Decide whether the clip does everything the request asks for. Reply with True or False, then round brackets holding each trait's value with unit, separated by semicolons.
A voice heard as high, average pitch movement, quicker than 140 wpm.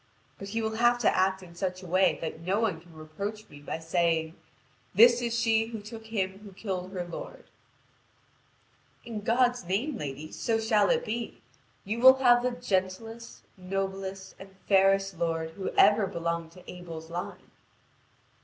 True (195 Hz; 4.2 semitones; 165 wpm)